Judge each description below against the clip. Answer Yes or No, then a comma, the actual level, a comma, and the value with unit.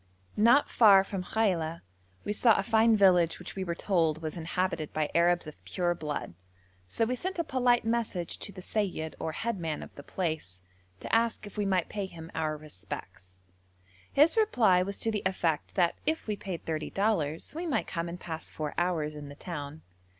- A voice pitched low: No, medium, 180 Hz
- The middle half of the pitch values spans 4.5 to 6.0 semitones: Yes, average, 5.1 semitones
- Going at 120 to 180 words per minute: No, average, 195 wpm